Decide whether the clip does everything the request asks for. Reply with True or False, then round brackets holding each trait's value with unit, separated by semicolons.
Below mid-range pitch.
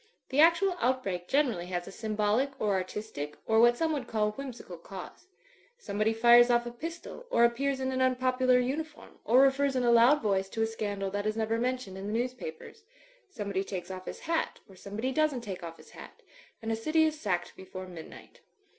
False (235 Hz)